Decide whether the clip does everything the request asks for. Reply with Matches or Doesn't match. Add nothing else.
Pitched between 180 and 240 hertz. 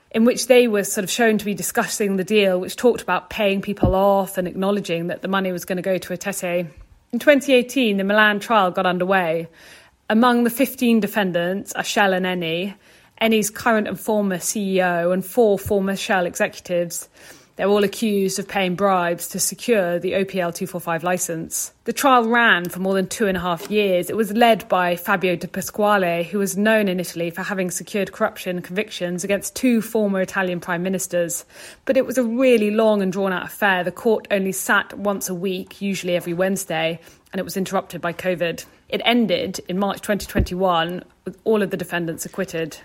Matches